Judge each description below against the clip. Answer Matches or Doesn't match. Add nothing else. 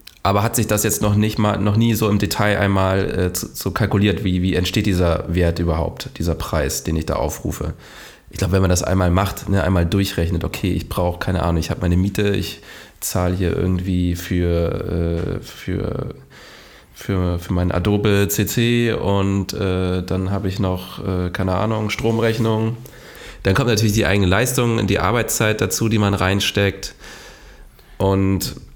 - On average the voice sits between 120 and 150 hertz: Doesn't match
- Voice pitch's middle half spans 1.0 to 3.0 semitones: Matches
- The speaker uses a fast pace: Doesn't match